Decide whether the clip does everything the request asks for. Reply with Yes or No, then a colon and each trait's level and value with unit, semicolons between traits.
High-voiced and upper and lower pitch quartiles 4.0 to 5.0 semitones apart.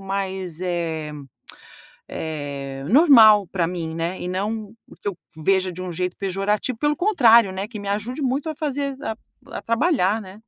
Yes: high, 200 Hz; average, 4.6 semitones